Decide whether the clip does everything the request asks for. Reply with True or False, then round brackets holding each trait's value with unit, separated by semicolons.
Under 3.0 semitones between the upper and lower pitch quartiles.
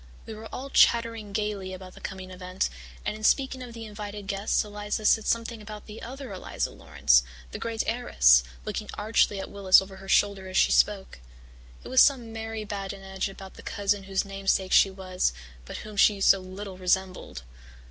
True (2.5 semitones)